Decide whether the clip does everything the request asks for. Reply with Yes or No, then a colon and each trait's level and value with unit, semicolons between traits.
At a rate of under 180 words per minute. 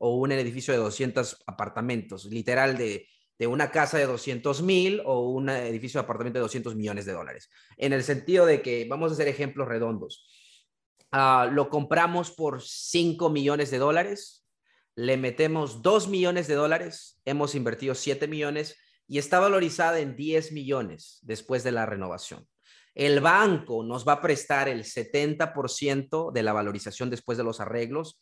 Yes: average, 165 wpm